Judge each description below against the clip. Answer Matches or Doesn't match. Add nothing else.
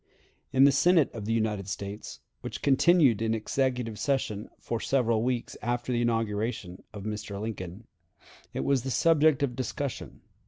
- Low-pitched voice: Matches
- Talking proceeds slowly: Doesn't match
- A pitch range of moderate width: Matches